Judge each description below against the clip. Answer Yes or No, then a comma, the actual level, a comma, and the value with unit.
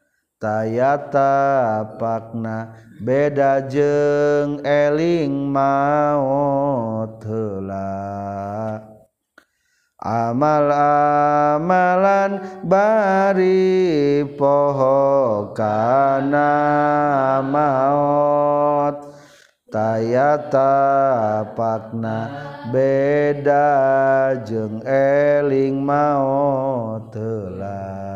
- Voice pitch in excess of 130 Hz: Yes, medium, 140 Hz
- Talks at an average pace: No, slow, 45 wpm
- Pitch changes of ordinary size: Yes, average, 4.6 semitones